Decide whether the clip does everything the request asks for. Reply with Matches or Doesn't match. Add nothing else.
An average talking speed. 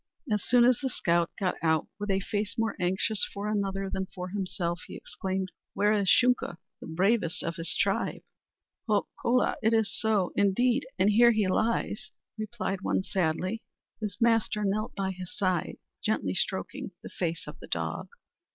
Matches